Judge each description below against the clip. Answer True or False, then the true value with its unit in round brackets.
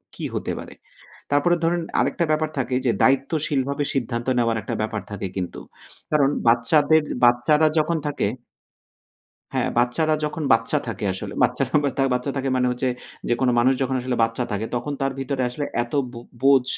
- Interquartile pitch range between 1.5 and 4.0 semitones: True (3.5 semitones)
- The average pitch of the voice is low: True (130 Hz)